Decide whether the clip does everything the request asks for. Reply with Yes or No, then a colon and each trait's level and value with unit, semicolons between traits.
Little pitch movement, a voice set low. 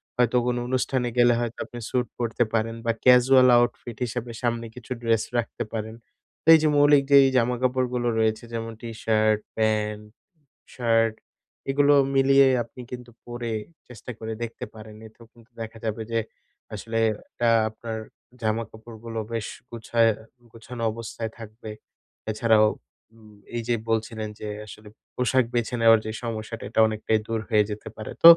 Yes: narrow, 1.8 semitones; low, 115 Hz